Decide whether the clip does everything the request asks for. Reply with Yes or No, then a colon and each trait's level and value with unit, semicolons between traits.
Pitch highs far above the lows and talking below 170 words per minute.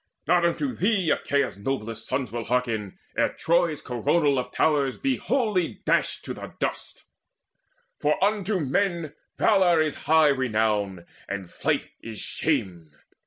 Yes: wide, 7.1 semitones; slow, 135 wpm